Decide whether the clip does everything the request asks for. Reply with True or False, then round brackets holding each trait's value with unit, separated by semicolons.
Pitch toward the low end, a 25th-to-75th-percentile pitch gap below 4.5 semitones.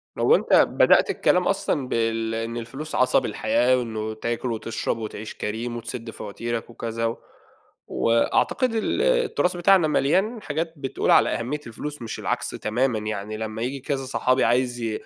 True (120 Hz; 3.6 semitones)